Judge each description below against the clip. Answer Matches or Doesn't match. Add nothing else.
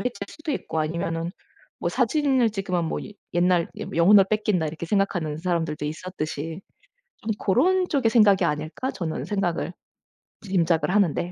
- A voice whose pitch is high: Doesn't match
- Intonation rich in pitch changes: Doesn't match